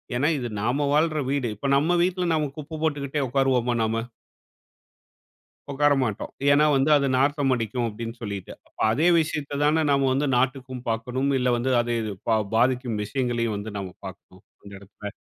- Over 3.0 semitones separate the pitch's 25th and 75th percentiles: Yes, average, 4.0 semitones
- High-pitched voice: No, low, 130 Hz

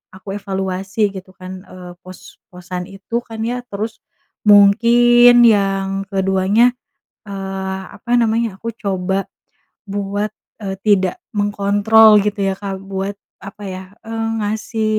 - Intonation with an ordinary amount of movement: No, narrow, 2.1 semitones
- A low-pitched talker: No, high, 200 Hz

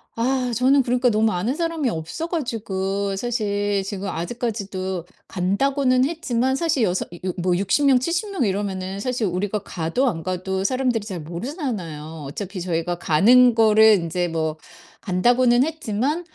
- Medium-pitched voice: No, high, 210 Hz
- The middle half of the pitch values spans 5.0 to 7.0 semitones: Yes, wide, 5.4 semitones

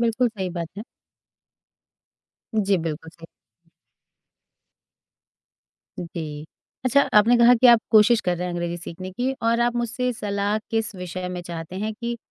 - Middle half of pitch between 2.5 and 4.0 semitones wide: No, average, 5.3 semitones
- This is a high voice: Yes, high, 205 Hz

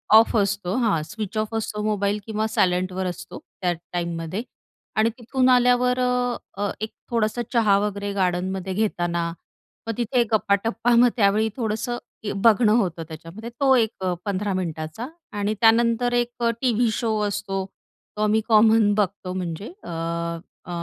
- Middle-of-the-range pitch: No, high, 210 Hz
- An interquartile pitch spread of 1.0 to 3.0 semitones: No, average, 3.7 semitones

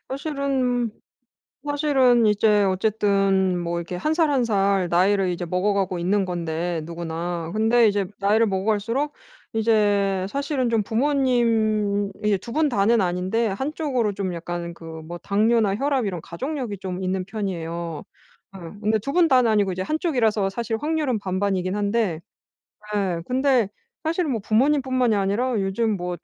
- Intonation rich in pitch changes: No, average, 4.7 semitones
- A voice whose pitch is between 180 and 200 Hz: No, high, 210 Hz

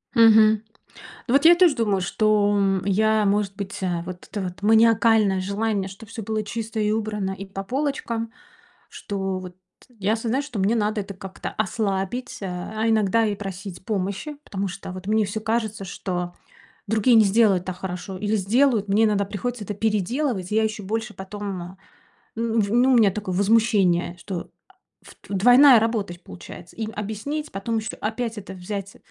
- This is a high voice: Yes, high, 210 Hz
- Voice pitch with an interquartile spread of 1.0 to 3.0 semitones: Yes, narrow, 2.6 semitones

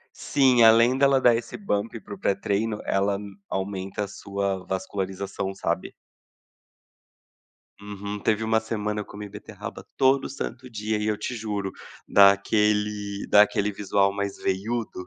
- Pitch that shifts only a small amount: Yes, narrow, 2.1 semitones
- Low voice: Yes, low, 105 Hz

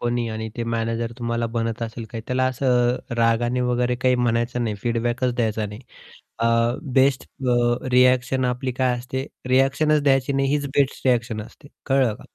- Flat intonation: Yes, narrow, 1.8 semitones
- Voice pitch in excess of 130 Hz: No, low, 125 Hz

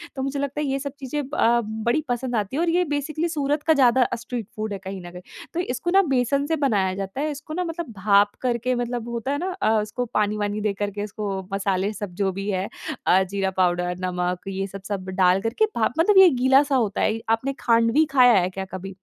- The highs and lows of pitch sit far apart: Yes, wide, 5.9 semitones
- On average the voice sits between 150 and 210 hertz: No, high, 230 Hz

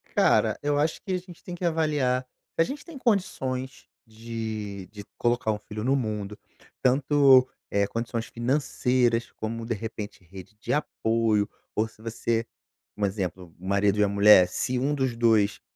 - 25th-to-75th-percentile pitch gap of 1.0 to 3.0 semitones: No, average, 4.2 semitones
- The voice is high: No, low, 115 Hz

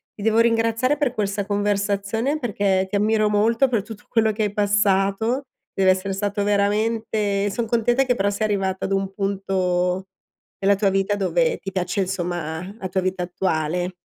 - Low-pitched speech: No, high, 200 Hz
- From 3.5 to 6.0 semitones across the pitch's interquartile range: No, narrow, 2.4 semitones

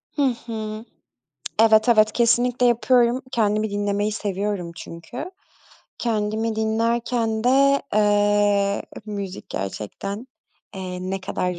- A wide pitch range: No, narrow, 2.5 semitones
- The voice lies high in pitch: Yes, high, 215 Hz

